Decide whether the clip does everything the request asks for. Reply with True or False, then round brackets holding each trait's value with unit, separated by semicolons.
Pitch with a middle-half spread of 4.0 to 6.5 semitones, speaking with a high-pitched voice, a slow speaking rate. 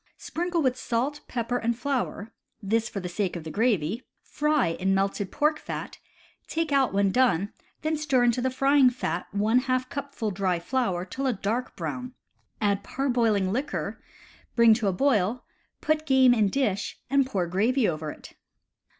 False (5.2 semitones; 235 Hz; 165 wpm)